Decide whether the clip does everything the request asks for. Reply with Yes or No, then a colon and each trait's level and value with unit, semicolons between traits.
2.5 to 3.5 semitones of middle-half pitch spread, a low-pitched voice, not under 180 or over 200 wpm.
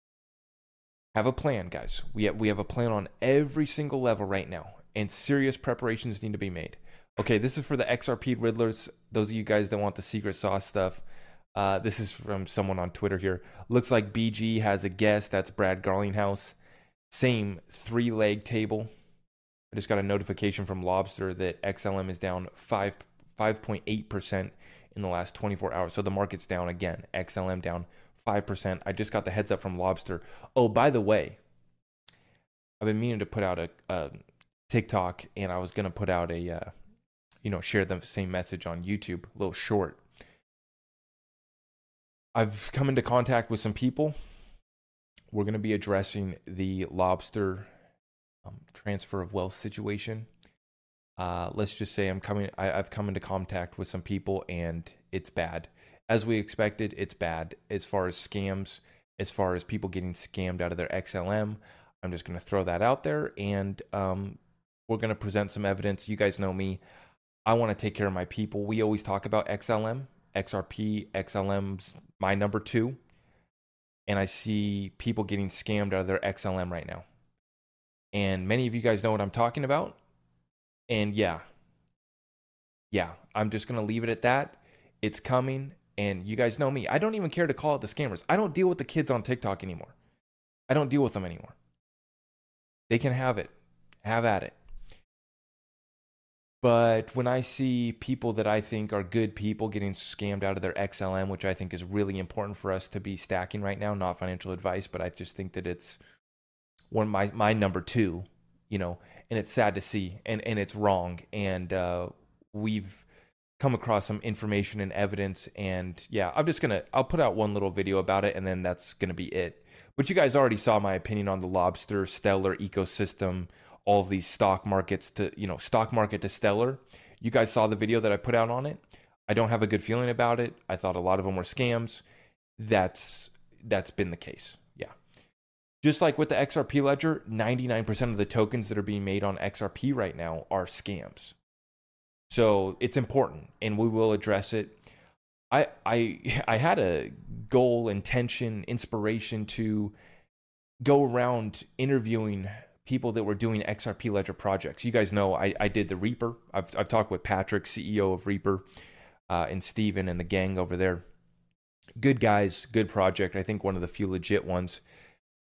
Yes: average, 3.0 semitones; low, 100 Hz; average, 185 wpm